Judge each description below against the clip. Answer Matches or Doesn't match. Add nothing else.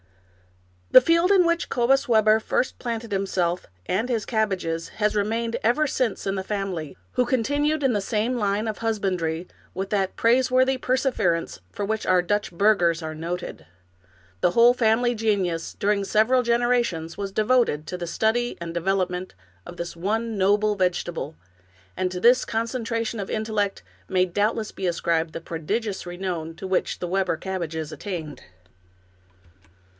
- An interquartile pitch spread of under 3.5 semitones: Doesn't match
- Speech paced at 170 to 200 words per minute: Doesn't match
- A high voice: Matches